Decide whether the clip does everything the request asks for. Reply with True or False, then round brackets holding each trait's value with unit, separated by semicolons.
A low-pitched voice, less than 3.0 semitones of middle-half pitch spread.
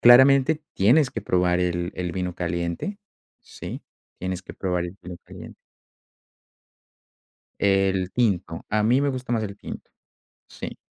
False (95 Hz; 5.4 semitones)